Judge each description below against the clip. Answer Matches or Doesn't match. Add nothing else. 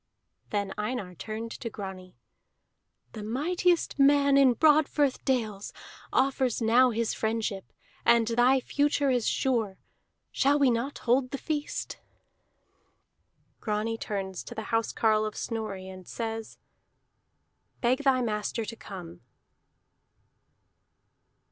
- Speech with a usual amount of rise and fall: Matches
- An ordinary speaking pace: Doesn't match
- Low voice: Doesn't match